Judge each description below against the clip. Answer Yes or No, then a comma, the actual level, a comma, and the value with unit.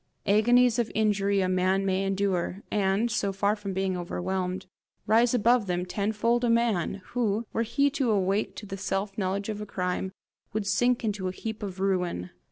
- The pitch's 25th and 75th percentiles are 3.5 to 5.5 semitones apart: No, narrow, 2.6 semitones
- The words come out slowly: No, average, 180 wpm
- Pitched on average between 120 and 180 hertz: No, high, 200 Hz